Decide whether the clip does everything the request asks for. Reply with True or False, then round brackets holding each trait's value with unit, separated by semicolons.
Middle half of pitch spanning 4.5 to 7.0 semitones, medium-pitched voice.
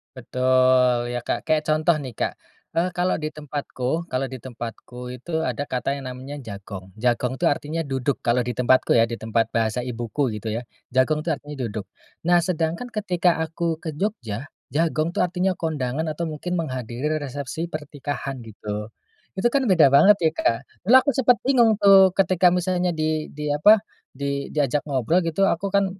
True (5.3 semitones; 145 Hz)